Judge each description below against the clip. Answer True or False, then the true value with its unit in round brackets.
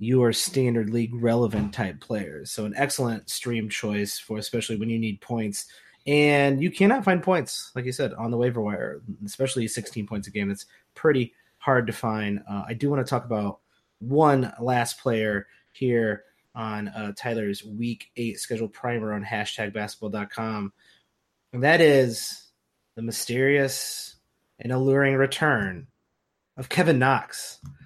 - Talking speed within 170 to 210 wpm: False (155 wpm)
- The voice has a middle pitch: False (115 Hz)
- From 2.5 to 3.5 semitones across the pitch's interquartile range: False (3.9 semitones)